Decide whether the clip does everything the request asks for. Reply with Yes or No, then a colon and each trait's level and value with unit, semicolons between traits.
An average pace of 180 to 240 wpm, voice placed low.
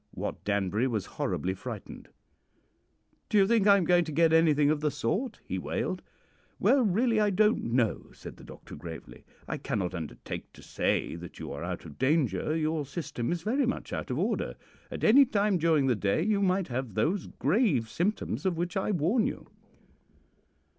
No: average, 185 wpm; medium, 160 Hz